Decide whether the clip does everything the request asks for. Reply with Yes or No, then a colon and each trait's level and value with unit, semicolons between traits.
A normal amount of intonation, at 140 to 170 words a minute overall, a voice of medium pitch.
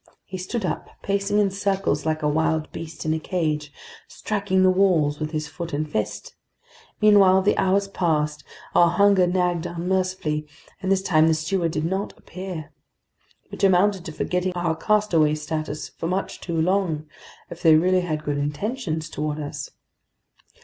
Yes: average, 3.6 semitones; average, 165 wpm; medium, 170 Hz